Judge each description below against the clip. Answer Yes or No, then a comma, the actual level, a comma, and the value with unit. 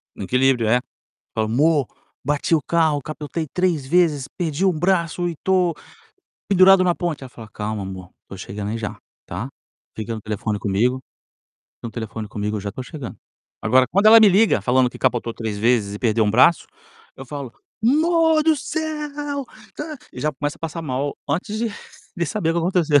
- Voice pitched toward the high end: No, medium, 145 Hz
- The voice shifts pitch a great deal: Yes, wide, 8.1 semitones